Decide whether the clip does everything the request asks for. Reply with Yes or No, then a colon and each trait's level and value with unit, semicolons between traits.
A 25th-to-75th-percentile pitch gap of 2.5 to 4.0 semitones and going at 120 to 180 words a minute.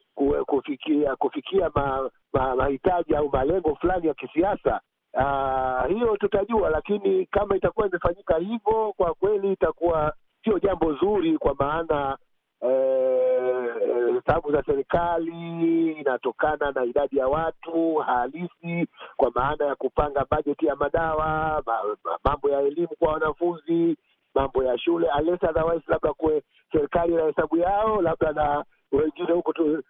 No: average, 4.4 semitones; average, 135 wpm